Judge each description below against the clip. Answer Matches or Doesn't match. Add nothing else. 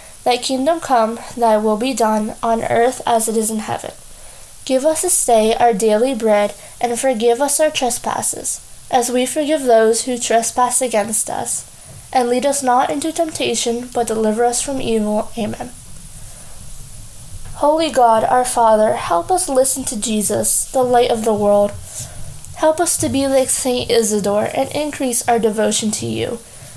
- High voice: Matches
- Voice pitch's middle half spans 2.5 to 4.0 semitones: Matches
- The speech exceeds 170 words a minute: Doesn't match